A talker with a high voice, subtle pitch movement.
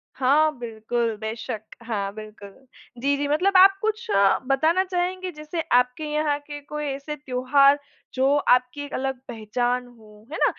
No: very high, 275 Hz; average, 4.0 semitones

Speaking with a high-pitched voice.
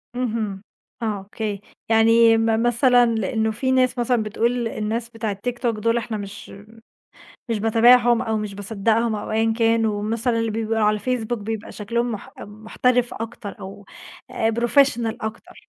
Yes: high, 225 Hz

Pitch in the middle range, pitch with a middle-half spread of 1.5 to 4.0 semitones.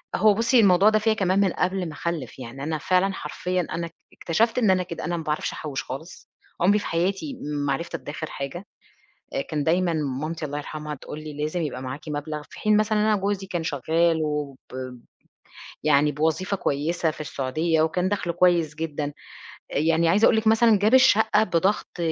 No: medium, 170 Hz; average, 4.4 semitones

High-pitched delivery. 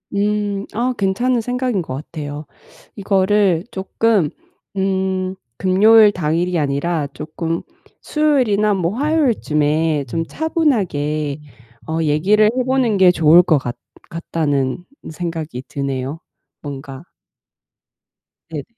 No: medium, 180 Hz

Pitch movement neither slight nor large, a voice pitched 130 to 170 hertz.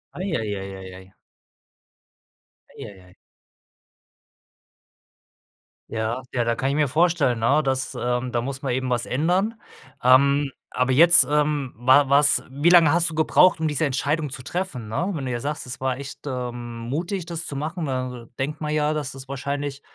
Yes: average, 3.7 semitones; medium, 140 Hz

